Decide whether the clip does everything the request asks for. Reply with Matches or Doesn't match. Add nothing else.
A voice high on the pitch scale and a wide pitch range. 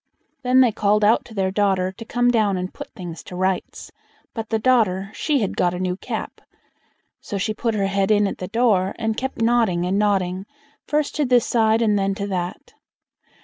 Doesn't match